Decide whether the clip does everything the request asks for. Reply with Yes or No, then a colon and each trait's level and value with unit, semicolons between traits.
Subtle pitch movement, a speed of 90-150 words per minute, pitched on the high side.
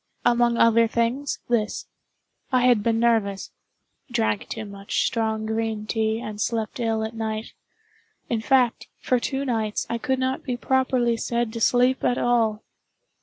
Yes: narrow, 2.0 semitones; average, 145 wpm; high, 230 Hz